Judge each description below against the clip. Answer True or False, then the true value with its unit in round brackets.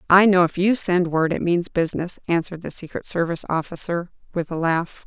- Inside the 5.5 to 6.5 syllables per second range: True (5.7 syllables/s)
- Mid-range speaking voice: True (175 Hz)